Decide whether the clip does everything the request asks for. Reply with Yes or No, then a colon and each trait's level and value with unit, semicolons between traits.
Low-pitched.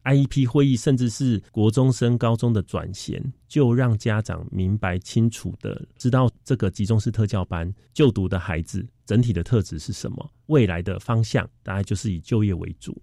Yes: low, 115 Hz